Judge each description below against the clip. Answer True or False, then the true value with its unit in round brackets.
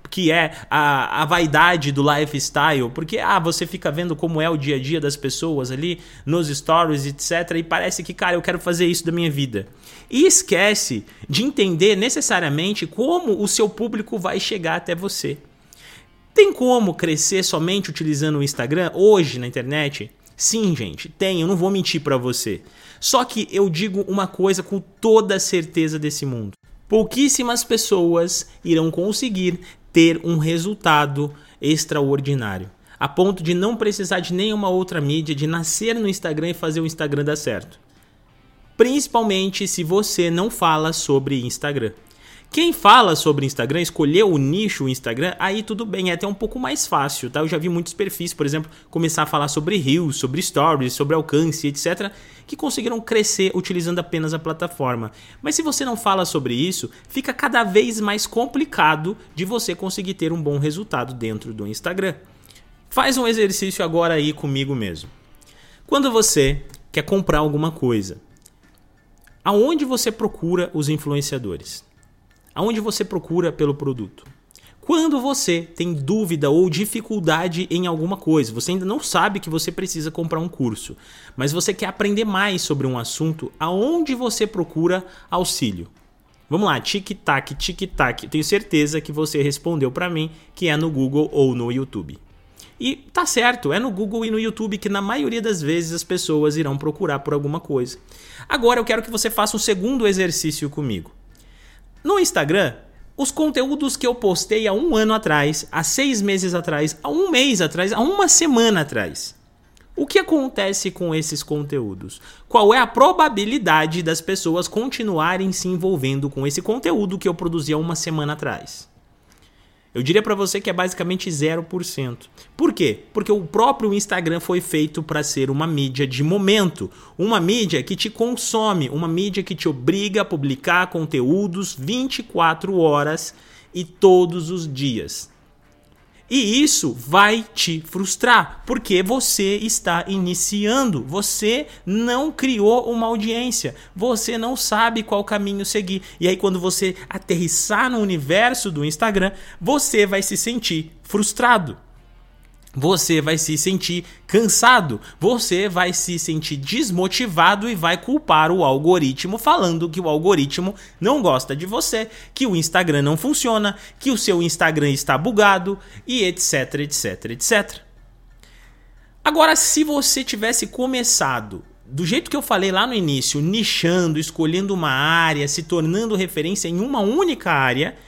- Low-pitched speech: False (180 Hz)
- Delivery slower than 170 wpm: True (155 wpm)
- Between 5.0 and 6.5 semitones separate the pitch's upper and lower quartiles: True (5.5 semitones)